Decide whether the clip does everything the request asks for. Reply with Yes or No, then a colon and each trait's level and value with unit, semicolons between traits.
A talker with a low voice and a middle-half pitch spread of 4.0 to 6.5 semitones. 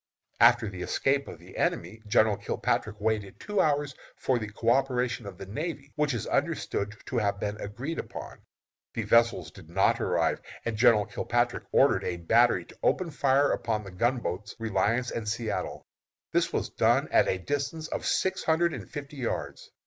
Yes: low, 115 Hz; average, 5.0 semitones